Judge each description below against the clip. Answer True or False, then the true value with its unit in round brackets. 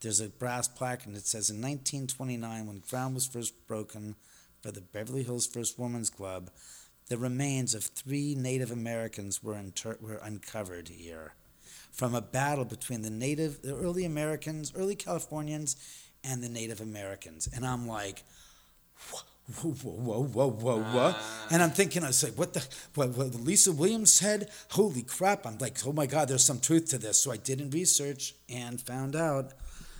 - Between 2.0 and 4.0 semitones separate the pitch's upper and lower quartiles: False (4.8 semitones)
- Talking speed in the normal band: True (180 wpm)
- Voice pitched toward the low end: True (125 Hz)